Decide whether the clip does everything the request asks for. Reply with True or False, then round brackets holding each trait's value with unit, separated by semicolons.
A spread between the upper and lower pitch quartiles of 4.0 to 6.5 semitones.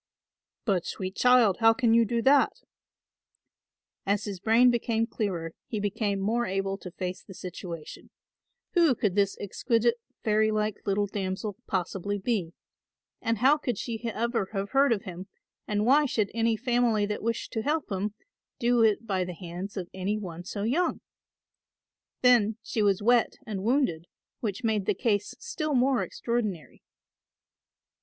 False (3.5 semitones)